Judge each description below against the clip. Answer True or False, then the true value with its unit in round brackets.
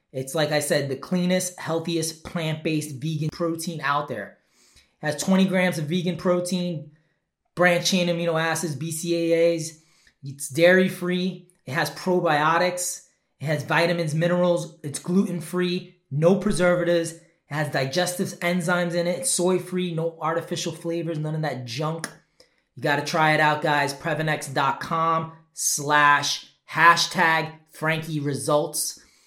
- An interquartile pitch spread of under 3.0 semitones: True (2.5 semitones)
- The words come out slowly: True (125 wpm)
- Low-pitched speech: False (165 Hz)